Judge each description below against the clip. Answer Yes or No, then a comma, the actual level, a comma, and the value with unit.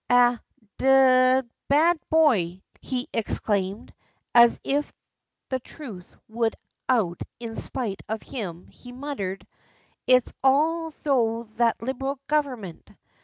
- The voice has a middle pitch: No, high, 245 Hz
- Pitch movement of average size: Yes, average, 3.7 semitones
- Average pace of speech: No, slow, 120 wpm